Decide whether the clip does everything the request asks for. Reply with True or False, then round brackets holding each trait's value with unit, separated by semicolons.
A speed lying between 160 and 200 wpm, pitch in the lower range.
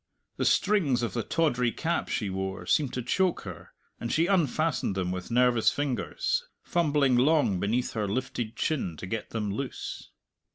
True (165 wpm; 125 Hz)